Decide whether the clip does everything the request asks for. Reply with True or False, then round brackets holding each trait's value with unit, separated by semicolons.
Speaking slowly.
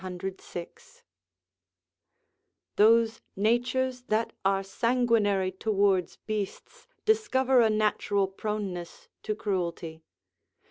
True (80 wpm)